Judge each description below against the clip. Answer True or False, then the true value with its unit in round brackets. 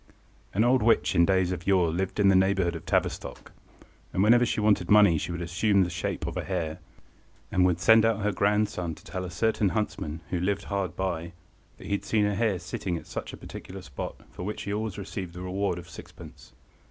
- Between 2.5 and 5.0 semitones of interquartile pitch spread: True (2.8 semitones)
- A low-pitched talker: True (95 Hz)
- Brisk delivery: True (220 wpm)